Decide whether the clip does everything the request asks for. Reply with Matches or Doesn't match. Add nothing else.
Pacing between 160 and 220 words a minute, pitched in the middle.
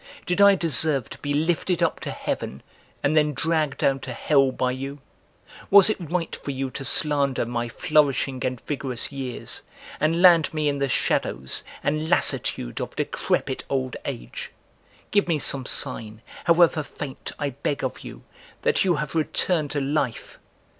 Matches